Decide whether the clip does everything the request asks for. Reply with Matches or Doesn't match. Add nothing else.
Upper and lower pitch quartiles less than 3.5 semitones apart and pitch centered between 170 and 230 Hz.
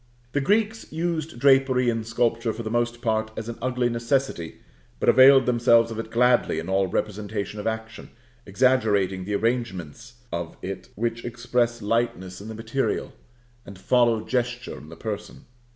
Doesn't match